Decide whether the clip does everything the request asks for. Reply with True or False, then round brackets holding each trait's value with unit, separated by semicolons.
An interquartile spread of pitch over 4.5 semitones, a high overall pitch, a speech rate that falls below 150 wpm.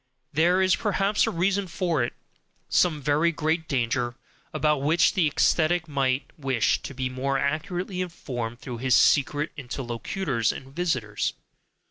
False (5.0 semitones; 150 Hz; 140 wpm)